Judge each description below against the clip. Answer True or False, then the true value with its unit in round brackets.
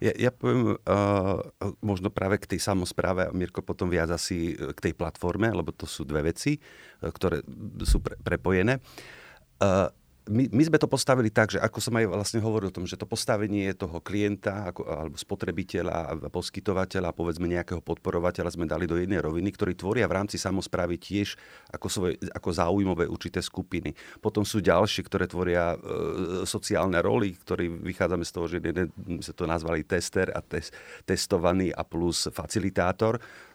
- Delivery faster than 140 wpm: True (165 wpm)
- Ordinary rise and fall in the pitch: True (3.1 semitones)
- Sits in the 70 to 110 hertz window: True (95 Hz)